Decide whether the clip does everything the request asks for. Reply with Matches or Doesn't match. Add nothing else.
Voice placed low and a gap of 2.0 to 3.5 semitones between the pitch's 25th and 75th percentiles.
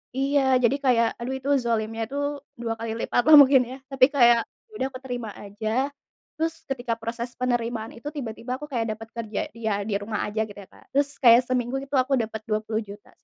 Doesn't match